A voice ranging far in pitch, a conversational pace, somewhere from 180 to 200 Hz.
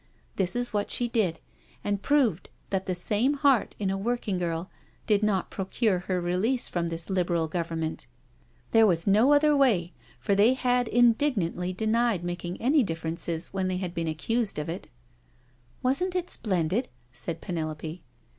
Yes: wide, 5.7 semitones; average, 165 wpm; high, 190 Hz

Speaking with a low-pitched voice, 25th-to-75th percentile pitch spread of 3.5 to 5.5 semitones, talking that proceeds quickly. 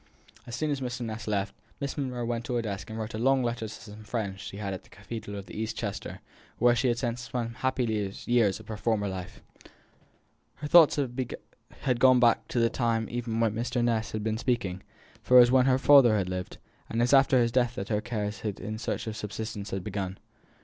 No: low, 115 Hz; average, 2.8 semitones; fast, 235 wpm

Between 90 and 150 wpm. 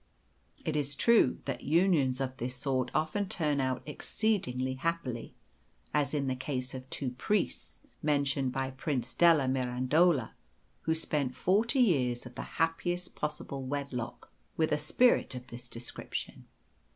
Yes: average, 140 wpm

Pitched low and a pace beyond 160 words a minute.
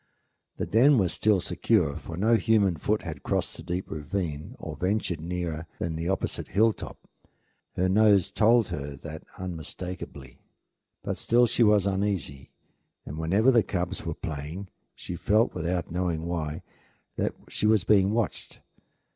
No: very low, 90 Hz; average, 150 wpm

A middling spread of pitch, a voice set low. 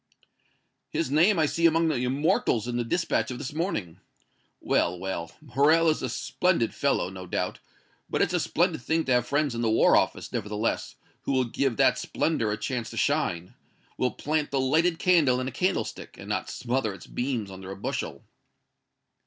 No: wide, 6.1 semitones; low, 130 Hz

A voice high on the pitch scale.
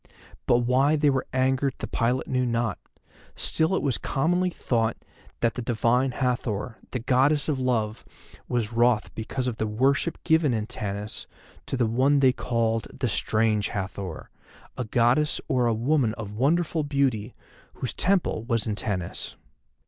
No: low, 125 Hz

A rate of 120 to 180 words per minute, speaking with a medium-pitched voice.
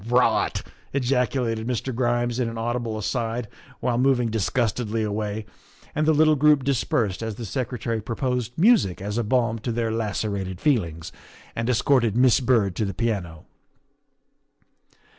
No: average, 150 wpm; low, 115 Hz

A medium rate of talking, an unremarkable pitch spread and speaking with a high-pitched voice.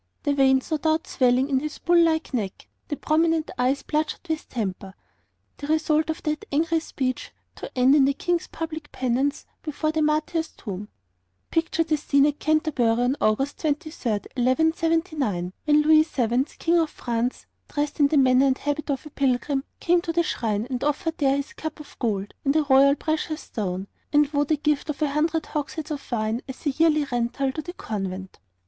Yes: average, 190 wpm; average, 3.6 semitones; very high, 290 Hz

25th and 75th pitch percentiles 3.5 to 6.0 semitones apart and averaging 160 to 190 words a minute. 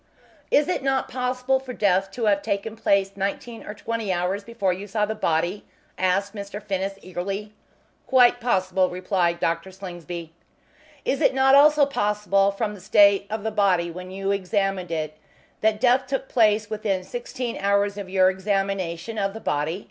No: average, 3.1 semitones; average, 170 wpm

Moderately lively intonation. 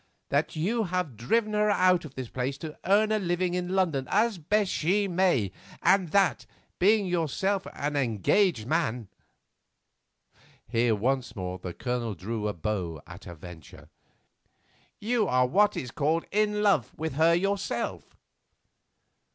No: wide, 8.3 semitones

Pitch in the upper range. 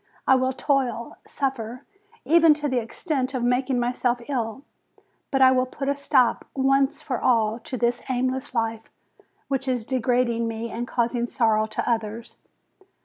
Yes: very high, 250 Hz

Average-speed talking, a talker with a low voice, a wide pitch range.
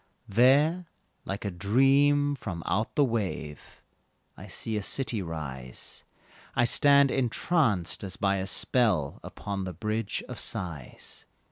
No: slow, 130 wpm; low, 105 Hz; wide, 6.8 semitones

